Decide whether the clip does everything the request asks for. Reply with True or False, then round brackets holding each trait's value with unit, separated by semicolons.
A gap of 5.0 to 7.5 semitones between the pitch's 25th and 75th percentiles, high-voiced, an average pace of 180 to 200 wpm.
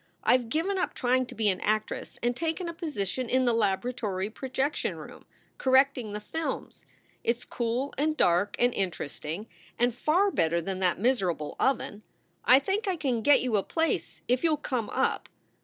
True (5.6 semitones; 245 Hz; 185 wpm)